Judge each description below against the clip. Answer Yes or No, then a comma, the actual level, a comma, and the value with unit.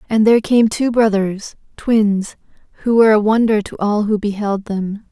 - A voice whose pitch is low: No, high, 215 Hz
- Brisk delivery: No, average, 175 wpm